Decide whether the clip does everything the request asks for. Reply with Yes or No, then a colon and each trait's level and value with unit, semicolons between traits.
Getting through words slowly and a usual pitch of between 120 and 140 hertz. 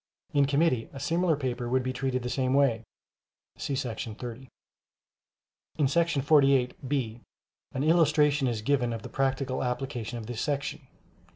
No: average, 155 wpm; low, 135 Hz